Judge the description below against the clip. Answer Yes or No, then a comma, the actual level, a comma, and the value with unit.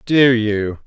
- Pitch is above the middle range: No, low, 115 Hz